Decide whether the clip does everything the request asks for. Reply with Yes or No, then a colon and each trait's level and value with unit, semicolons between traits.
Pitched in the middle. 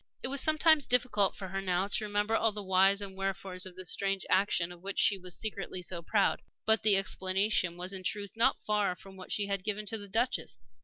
No: high, 195 Hz